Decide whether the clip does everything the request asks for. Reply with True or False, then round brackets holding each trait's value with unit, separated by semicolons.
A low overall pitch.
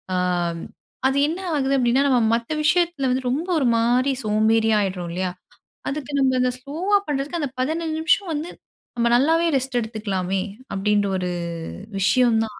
False (255 Hz)